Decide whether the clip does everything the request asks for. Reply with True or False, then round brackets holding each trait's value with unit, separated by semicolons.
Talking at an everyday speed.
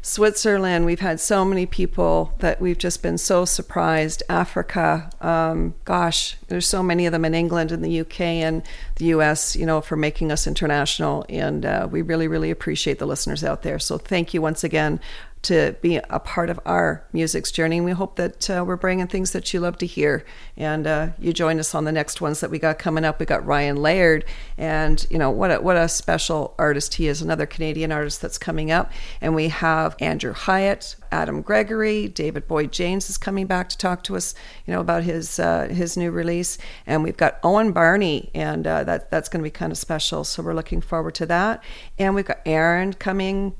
False (215 wpm)